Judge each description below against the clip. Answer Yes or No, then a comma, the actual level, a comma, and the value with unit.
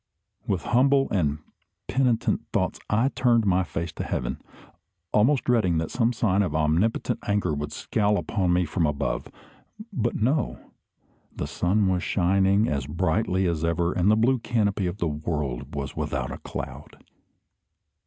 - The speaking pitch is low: Yes, very low, 95 Hz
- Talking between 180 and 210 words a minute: No, average, 155 wpm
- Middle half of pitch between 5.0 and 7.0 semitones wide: Yes, average, 5.3 semitones